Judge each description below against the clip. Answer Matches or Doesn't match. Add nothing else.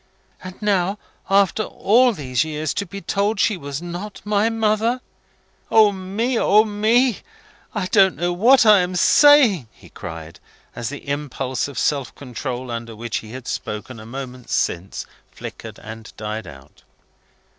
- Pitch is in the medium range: Matches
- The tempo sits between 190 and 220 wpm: Doesn't match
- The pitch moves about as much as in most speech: Doesn't match